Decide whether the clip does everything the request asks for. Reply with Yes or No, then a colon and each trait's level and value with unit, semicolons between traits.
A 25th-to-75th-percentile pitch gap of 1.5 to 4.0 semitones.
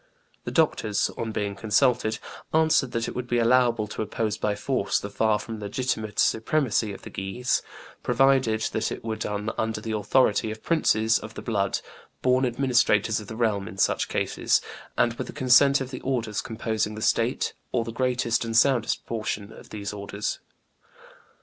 Yes: average, 2.8 semitones